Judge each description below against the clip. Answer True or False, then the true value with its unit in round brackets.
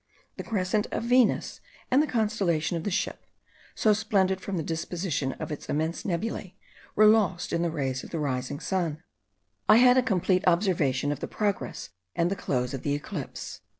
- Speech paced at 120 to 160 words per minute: False (185 wpm)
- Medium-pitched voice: True (180 Hz)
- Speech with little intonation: False (5.4 semitones)